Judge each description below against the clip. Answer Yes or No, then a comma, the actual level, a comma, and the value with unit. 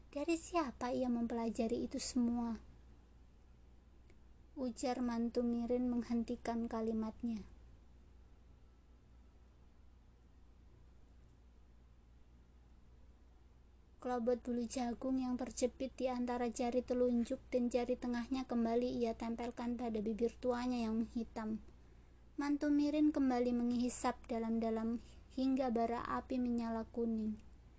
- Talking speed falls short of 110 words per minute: Yes, average, 90 wpm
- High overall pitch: Yes, high, 235 Hz